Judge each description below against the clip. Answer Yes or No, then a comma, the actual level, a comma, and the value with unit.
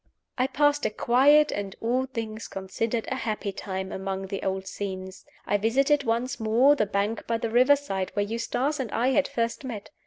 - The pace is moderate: Yes, average, 190 wpm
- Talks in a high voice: Yes, high, 230 Hz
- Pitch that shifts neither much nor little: Yes, average, 4.7 semitones